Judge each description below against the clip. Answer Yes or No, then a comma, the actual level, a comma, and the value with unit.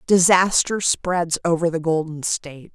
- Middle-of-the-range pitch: Yes, medium, 170 Hz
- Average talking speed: No, slow, 130 wpm